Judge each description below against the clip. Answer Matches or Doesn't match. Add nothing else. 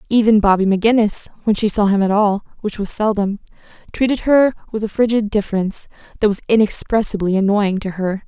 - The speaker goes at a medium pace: Matches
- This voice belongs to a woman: Matches